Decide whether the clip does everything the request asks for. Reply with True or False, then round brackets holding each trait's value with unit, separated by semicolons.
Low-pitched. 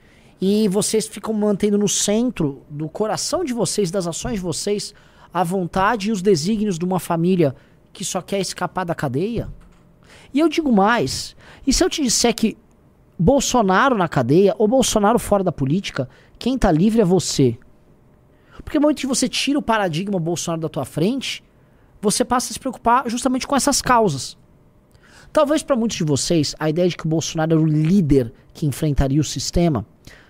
False (195 Hz)